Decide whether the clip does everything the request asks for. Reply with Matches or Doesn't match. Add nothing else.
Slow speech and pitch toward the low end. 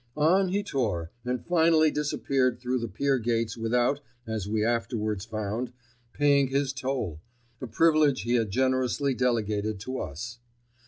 Doesn't match